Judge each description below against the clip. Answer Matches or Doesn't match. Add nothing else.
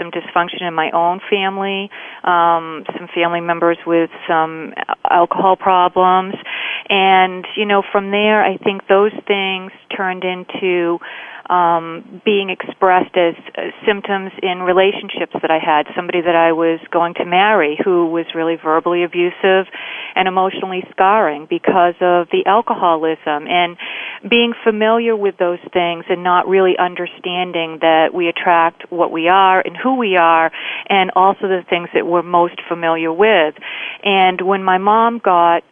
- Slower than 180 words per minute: Matches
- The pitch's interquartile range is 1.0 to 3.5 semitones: Matches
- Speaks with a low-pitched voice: Doesn't match